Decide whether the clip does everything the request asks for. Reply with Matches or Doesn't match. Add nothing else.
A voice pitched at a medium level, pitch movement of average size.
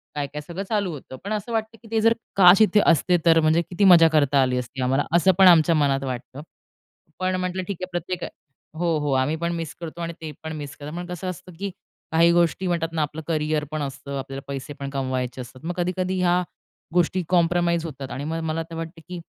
Matches